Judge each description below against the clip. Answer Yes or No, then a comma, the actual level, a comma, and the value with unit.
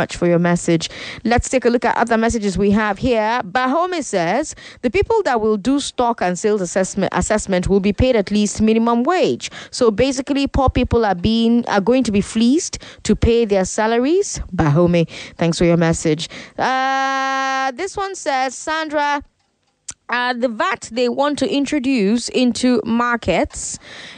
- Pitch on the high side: Yes, high, 235 Hz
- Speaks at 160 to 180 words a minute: Yes, average, 165 wpm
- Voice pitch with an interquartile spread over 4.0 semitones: Yes, average, 4.9 semitones